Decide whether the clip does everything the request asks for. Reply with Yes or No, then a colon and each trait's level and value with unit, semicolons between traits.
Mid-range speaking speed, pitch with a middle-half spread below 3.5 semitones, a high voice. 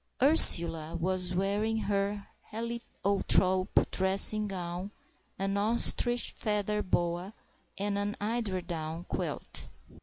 No: slow, 90 wpm; narrow, 2.6 semitones; high, 200 Hz